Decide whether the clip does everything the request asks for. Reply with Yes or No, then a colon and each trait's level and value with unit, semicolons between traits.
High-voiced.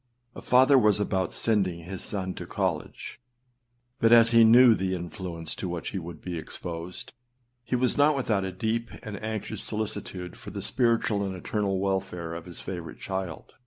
No: very low, 95 Hz